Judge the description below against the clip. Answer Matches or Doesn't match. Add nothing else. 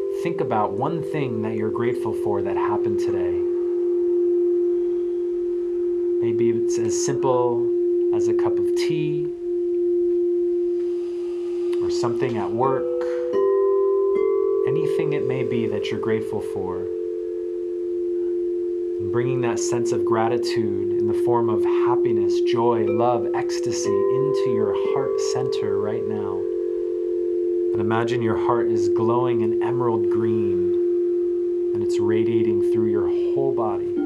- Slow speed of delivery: Matches